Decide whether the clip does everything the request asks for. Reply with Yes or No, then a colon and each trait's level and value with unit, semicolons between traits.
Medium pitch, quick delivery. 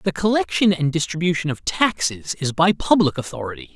No: medium, 165 Hz; average, 160 wpm